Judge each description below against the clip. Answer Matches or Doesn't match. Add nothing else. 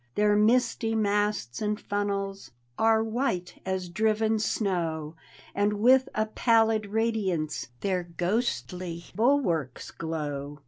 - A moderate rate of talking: Doesn't match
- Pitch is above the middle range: Matches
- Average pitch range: Matches